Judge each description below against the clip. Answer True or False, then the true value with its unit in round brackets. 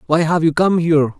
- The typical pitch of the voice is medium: True (160 Hz)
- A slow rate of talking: False (250 wpm)